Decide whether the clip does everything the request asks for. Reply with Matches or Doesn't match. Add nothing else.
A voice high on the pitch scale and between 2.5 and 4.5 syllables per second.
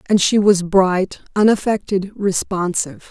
Matches